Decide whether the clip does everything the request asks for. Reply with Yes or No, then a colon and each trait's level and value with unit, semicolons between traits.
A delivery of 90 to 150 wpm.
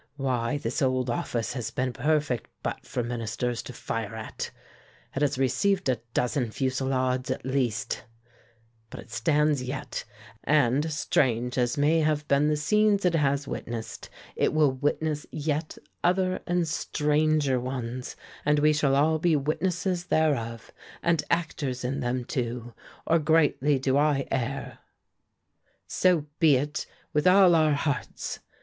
Yes: average, 145 wpm